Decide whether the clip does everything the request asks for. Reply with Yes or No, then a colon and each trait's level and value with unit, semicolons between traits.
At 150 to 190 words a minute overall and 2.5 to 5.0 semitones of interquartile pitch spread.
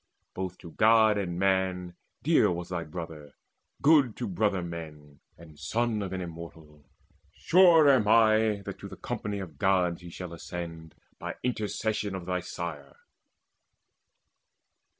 No: average, 140 wpm; average, 4.2 semitones